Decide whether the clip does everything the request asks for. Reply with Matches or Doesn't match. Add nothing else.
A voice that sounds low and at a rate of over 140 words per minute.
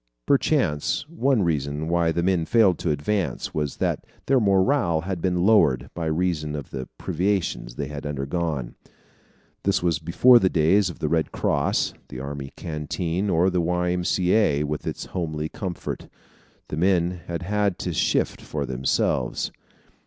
Matches